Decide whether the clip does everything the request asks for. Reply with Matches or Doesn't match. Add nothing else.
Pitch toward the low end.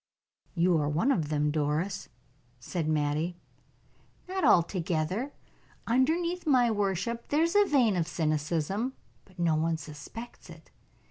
Doesn't match